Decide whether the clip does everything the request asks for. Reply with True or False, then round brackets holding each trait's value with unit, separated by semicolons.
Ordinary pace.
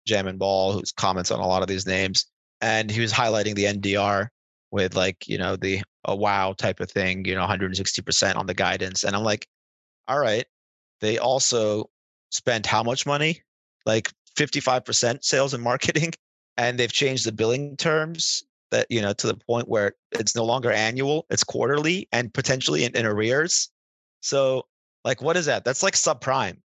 True (185 wpm)